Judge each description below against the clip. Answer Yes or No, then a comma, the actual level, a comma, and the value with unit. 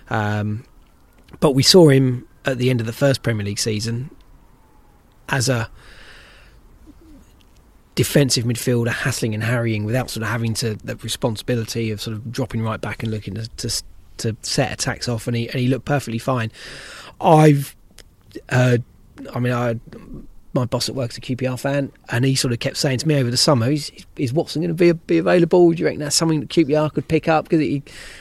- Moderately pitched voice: No, low, 125 Hz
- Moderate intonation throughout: Yes, average, 3.7 semitones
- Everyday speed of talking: Yes, average, 195 wpm